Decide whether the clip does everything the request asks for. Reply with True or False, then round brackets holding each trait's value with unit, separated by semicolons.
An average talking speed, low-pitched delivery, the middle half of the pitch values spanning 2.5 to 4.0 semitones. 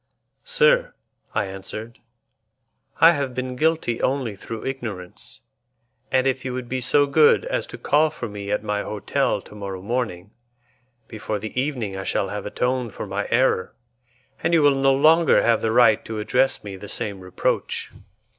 False (170 wpm; 120 Hz; 4.7 semitones)